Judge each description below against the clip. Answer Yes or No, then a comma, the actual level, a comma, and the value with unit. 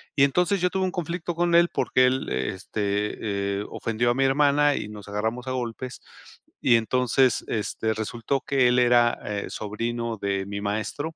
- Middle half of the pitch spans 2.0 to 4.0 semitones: No, average, 4.8 semitones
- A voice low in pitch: Yes, low, 120 Hz